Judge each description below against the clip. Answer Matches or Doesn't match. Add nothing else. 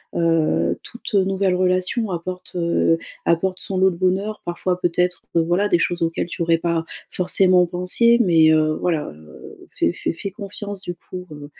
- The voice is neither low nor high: Matches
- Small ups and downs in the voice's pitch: Matches